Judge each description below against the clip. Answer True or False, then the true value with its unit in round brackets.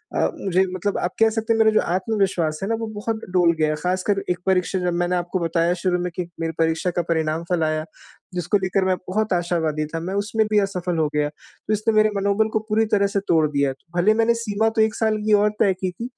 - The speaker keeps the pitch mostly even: False (3.9 semitones)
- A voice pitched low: False (185 Hz)